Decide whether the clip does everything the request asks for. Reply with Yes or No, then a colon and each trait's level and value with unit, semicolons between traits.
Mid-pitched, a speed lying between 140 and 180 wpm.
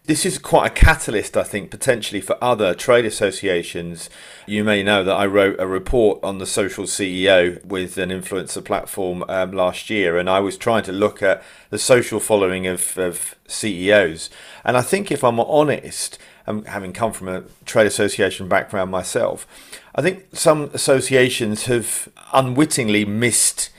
No: low, 105 Hz; average, 165 wpm